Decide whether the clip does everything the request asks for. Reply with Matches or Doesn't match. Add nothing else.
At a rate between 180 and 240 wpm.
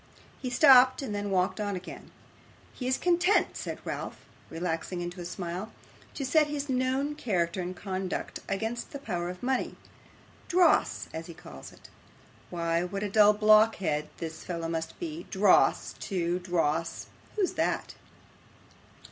Doesn't match